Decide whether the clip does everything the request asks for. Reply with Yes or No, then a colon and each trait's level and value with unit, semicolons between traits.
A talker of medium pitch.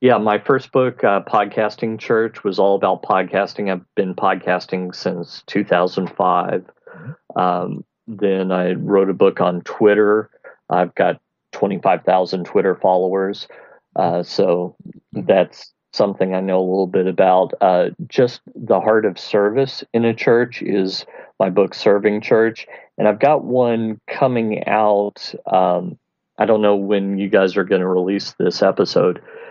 No: low, 100 Hz